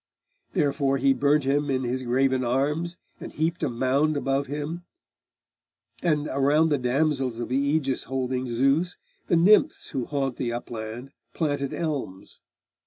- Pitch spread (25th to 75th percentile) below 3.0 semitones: Yes, narrow, 2.6 semitones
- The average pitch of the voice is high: No, low, 135 Hz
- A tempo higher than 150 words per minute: No, average, 145 wpm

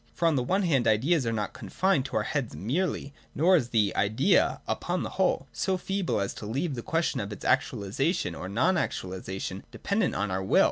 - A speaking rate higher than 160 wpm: Yes, fast, 205 wpm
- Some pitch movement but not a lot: No, wide, 8.7 semitones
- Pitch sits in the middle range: No, low, 130 Hz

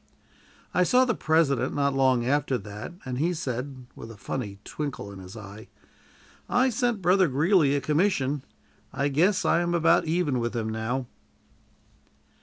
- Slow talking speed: No, average, 160 wpm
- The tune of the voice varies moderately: No, wide, 5.8 semitones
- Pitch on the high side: No, medium, 140 Hz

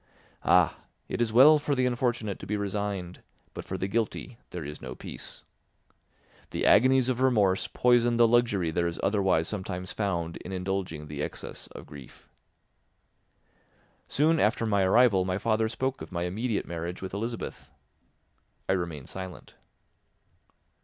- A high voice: No, low, 100 Hz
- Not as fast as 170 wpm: Yes, average, 150 wpm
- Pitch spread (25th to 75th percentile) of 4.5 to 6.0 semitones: Yes, average, 4.8 semitones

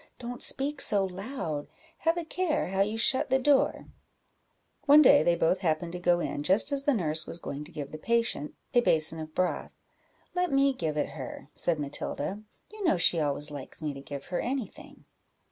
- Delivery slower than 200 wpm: No, fast, 205 wpm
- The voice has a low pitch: No, medium, 185 Hz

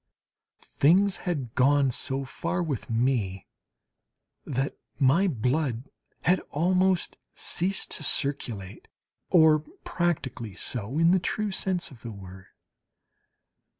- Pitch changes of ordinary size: No, wide, 6.4 semitones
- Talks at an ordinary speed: No, slow, 110 wpm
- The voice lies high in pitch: No, medium, 140 Hz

